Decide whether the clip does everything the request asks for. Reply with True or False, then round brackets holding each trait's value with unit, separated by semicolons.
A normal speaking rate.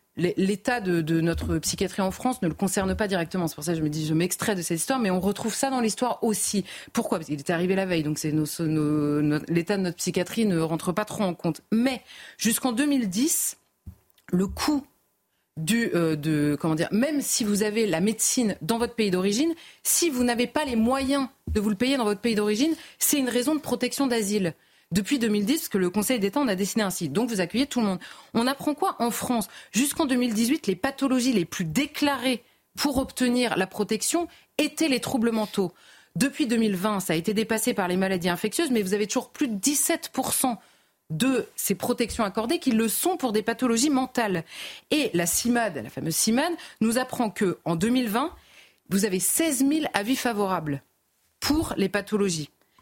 True (200 wpm)